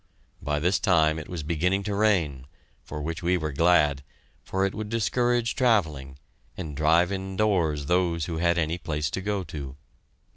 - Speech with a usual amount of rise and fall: Yes, average, 4.1 semitones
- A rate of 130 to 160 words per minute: No, average, 170 wpm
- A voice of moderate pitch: No, very low, 85 Hz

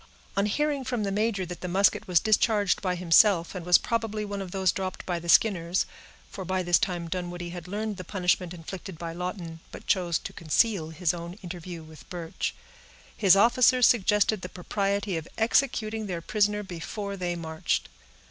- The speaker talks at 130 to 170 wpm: No, average, 180 wpm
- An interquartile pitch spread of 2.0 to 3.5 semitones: Yes, average, 3.2 semitones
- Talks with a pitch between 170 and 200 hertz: Yes, medium, 185 Hz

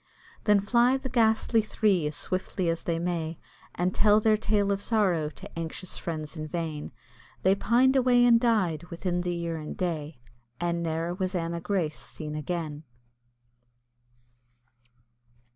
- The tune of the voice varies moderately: Yes, average, 4.4 semitones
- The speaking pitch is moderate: Yes, medium, 175 Hz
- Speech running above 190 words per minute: No, average, 145 wpm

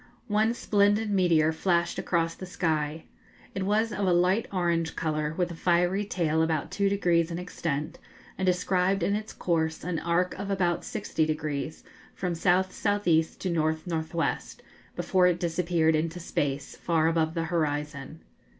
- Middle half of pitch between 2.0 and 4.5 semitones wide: Yes, average, 2.7 semitones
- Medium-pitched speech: Yes, medium, 170 Hz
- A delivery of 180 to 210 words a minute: No, average, 150 wpm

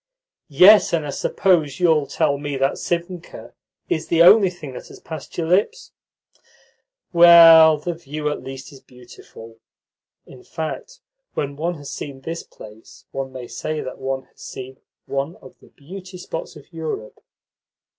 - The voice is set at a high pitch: No, medium, 155 Hz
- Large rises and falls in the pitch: No, average, 4.0 semitones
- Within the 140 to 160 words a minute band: Yes, average, 155 wpm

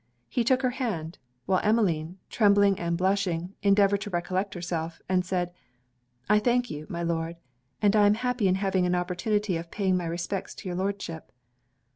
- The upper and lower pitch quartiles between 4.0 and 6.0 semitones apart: No, average, 3.0 semitones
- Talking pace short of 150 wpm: No, average, 175 wpm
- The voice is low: No, high, 190 Hz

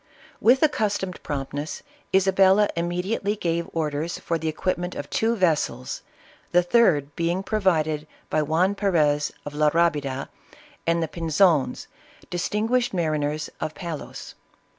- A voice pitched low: No, medium, 170 Hz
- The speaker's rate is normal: No, slow, 130 wpm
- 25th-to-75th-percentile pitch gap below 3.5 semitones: No, average, 4.0 semitones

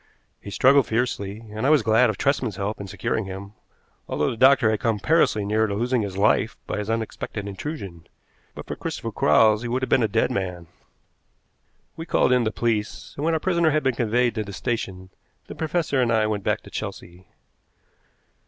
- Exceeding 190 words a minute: Yes, average, 200 wpm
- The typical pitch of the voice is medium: No, low, 110 Hz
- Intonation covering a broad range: No, average, 4.0 semitones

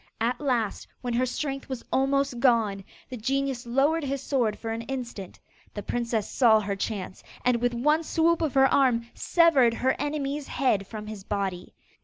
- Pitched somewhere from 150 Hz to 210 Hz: No, high, 245 Hz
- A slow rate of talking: No, average, 175 wpm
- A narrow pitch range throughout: No, average, 3.5 semitones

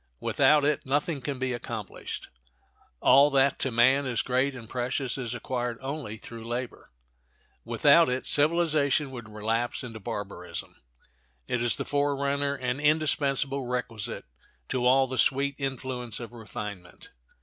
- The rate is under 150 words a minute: Yes, average, 140 wpm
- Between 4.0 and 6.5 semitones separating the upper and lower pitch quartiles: No, average, 2.9 semitones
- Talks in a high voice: No, low, 130 Hz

